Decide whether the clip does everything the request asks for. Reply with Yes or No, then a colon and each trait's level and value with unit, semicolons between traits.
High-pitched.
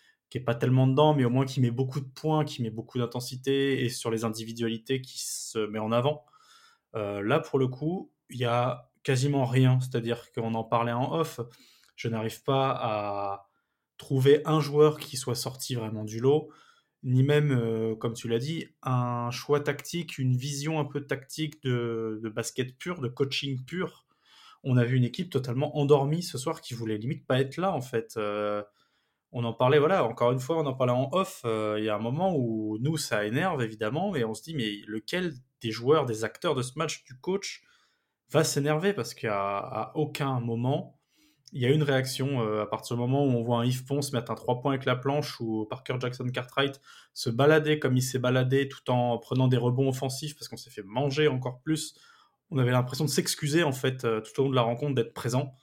No: low, 130 Hz